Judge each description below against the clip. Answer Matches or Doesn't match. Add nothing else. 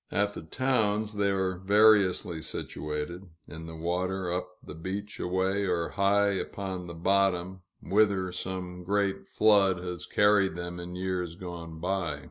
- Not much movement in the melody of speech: Matches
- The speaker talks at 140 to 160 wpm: Matches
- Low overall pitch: Matches